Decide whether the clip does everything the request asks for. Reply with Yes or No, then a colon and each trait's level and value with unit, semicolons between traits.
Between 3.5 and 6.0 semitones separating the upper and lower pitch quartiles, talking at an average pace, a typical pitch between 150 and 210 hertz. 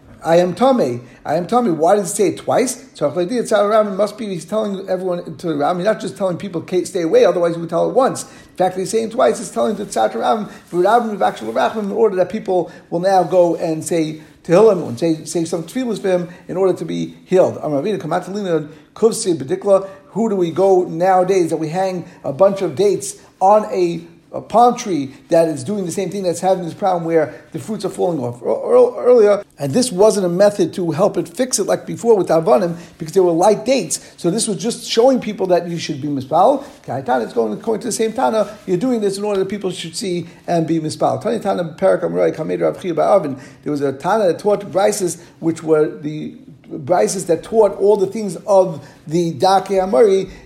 No: average, 3.9 semitones; fast, 210 wpm; medium, 185 Hz